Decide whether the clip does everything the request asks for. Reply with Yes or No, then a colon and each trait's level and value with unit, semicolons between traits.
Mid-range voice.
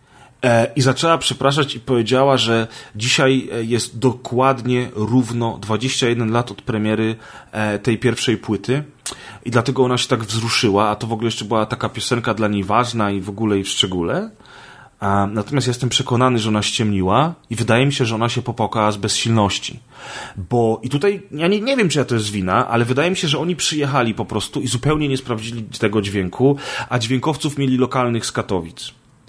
No: low, 120 Hz